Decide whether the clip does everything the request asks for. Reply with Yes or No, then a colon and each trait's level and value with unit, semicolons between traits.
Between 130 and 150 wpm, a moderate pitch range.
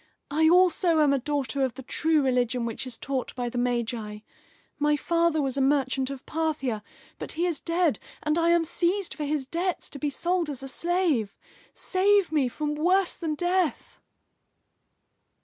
No: average, 175 wpm; average, 4.5 semitones